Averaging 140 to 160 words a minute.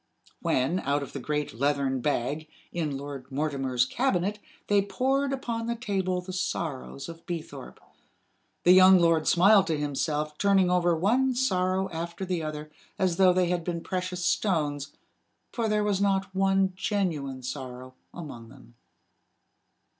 Yes: average, 145 wpm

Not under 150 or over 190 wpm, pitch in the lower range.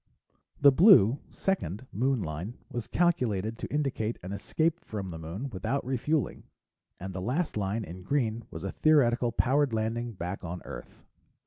Yes: average, 155 wpm; low, 115 Hz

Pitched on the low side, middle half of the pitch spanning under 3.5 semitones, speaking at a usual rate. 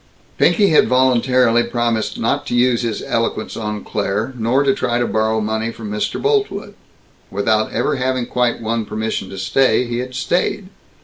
Yes: low, 120 Hz; average, 2.7 semitones; average, 170 wpm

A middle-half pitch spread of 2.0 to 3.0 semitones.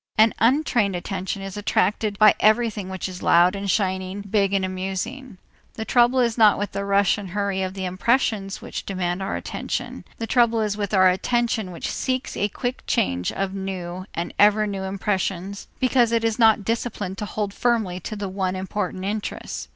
Yes: average, 2.7 semitones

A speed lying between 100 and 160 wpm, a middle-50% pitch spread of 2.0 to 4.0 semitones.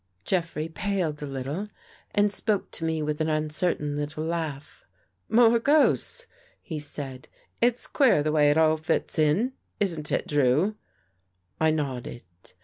No: average, 155 wpm; average, 5.1 semitones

